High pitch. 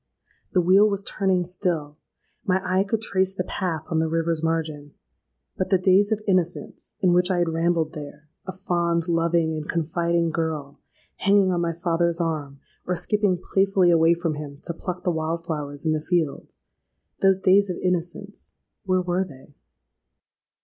No: medium, 170 Hz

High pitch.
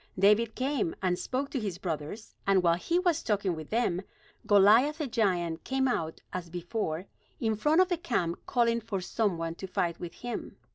Yes: high, 205 Hz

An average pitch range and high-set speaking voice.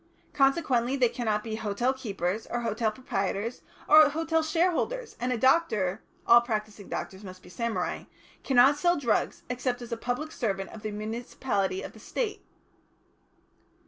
Yes: average, 4.3 semitones; high, 240 Hz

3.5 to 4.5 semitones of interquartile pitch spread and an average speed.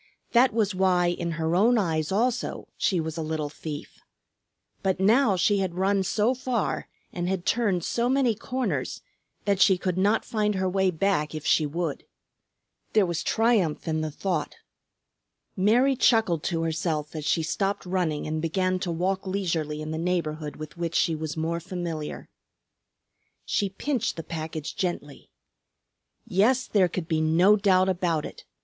Yes: average, 4.0 semitones; average, 165 wpm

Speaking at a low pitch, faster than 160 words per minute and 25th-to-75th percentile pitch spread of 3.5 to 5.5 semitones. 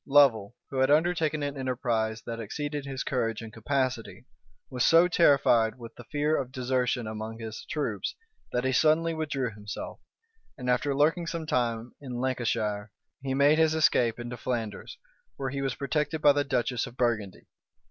Yes: low, 130 Hz; average, 170 wpm; average, 4.0 semitones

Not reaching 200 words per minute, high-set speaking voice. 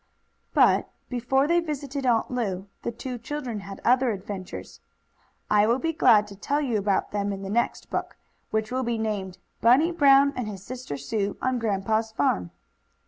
Yes: average, 175 wpm; high, 230 Hz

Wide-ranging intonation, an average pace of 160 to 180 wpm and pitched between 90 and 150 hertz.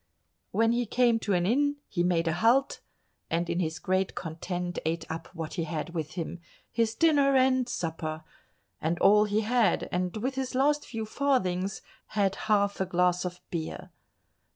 No: wide, 5.7 semitones; average, 165 wpm; high, 190 Hz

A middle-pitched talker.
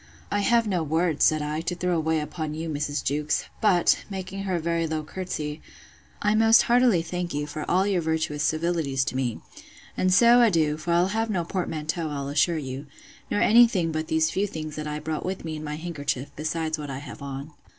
Yes: medium, 160 Hz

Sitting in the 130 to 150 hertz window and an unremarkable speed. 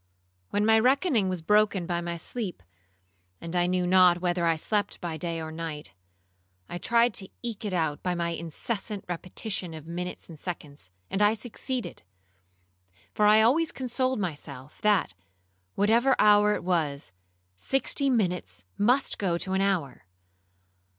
No: medium, 185 Hz; average, 155 wpm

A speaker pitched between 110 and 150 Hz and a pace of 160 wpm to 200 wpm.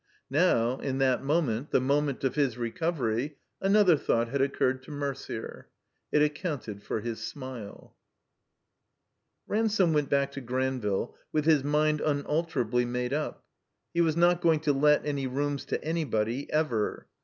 No: medium, 140 Hz; average, 150 wpm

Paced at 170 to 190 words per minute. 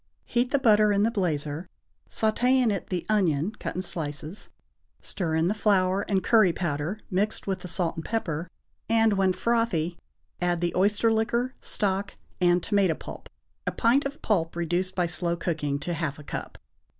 Yes: average, 175 wpm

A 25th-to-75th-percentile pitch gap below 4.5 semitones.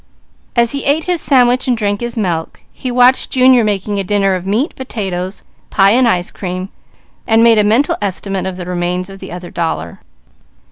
No: average, 5.0 semitones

